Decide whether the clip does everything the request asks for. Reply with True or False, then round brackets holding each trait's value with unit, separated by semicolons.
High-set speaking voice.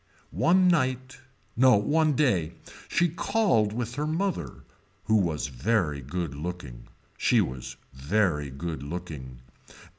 False (100 Hz)